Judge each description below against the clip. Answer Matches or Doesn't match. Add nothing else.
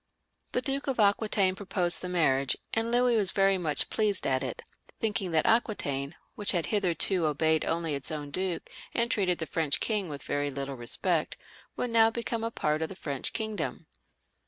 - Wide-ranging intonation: Matches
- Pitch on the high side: Doesn't match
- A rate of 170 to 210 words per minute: Matches